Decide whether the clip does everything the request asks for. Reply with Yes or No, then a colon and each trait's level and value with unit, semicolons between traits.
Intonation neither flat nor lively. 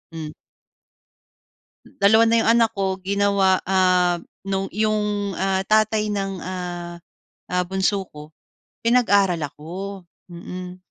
No: narrow, 2.0 semitones